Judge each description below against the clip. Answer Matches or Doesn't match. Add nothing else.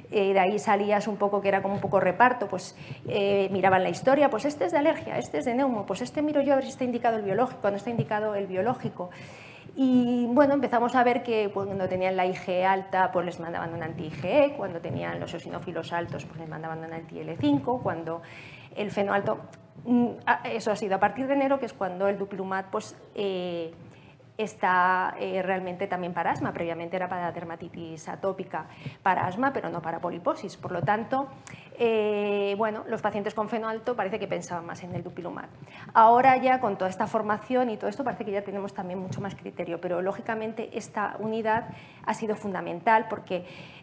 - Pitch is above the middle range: Matches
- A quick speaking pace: Matches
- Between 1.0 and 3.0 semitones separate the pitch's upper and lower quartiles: Doesn't match